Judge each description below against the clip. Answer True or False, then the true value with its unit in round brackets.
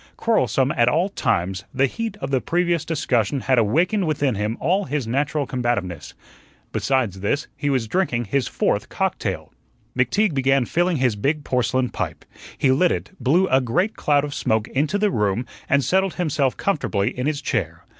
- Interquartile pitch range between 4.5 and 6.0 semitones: True (5.4 semitones)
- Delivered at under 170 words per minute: False (175 wpm)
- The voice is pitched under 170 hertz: True (135 Hz)